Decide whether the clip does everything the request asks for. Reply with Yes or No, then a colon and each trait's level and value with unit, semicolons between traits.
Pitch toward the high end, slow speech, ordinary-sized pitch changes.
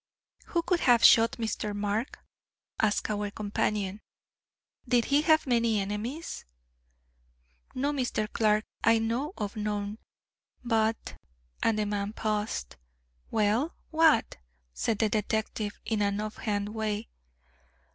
No: high, 215 Hz; slow, 125 wpm; narrow, 2.1 semitones